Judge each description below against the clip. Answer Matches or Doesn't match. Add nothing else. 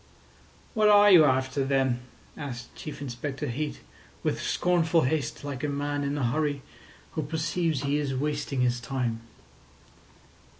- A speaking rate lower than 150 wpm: Matches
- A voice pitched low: Doesn't match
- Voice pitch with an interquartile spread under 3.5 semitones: Matches